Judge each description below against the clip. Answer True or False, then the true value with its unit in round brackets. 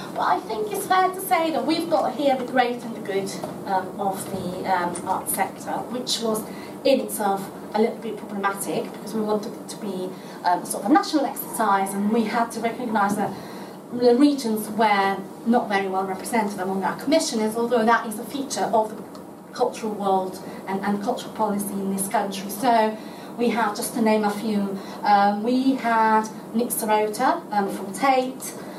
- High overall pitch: True (220 Hz)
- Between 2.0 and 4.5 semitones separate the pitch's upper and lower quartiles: True (3.3 semitones)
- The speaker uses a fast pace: False (190 wpm)